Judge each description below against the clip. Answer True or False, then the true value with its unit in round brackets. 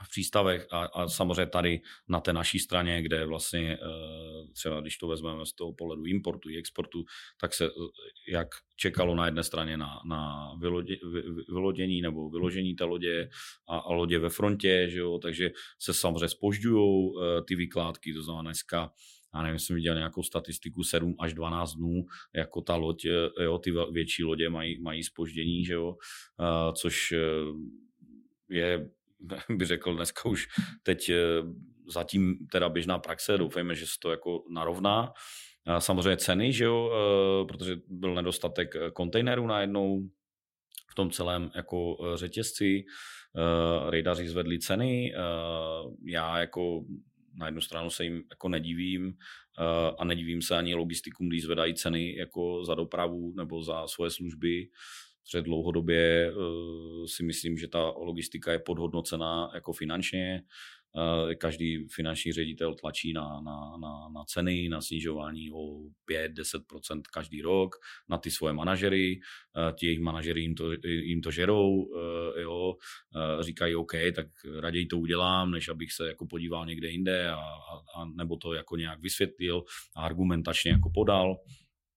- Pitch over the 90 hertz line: False (85 Hz)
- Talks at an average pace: True (150 wpm)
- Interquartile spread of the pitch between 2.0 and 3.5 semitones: False (1.5 semitones)